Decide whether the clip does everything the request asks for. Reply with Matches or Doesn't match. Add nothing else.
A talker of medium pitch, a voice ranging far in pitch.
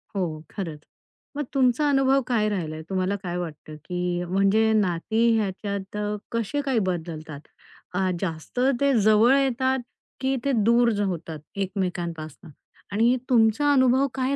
Doesn't match